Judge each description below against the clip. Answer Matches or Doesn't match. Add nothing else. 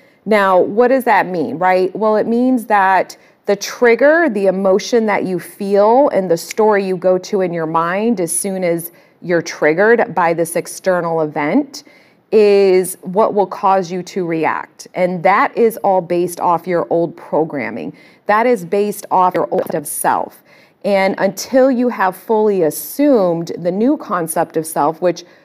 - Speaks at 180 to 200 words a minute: Doesn't match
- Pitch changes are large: Doesn't match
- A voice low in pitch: Doesn't match